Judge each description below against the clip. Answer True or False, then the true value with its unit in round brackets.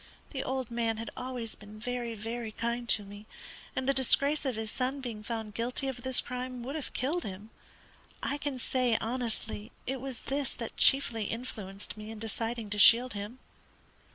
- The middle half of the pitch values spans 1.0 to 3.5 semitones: True (2.9 semitones)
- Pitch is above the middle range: True (235 Hz)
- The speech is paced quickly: False (180 wpm)